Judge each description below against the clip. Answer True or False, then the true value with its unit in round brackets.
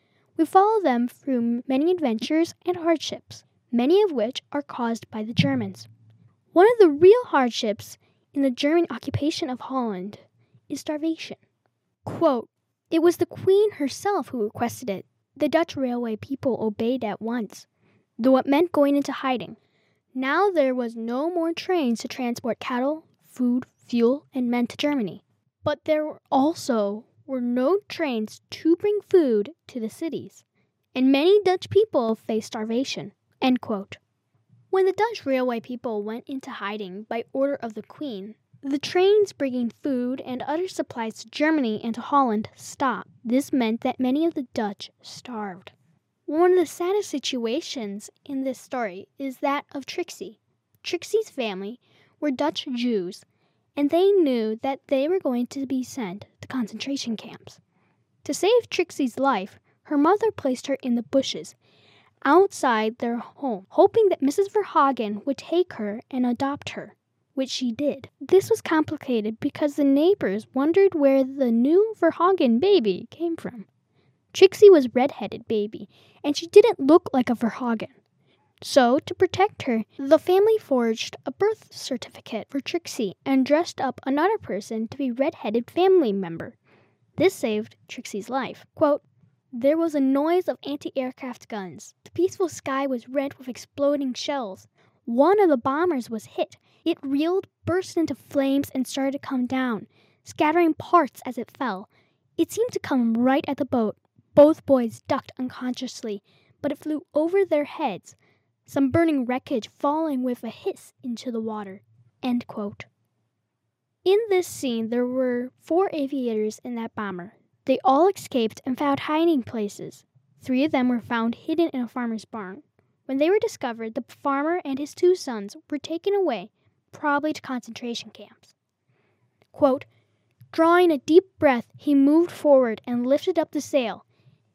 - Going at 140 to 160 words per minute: True (155 wpm)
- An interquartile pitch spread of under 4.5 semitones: False (5.3 semitones)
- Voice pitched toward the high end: True (270 Hz)